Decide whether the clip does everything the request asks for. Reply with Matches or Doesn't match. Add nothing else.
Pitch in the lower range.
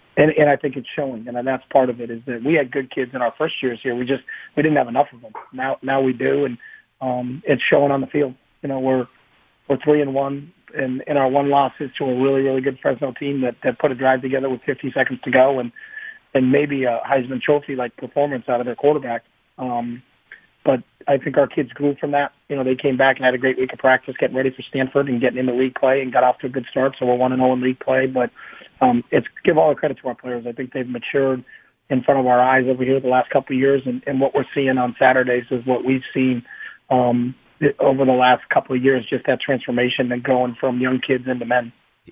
Matches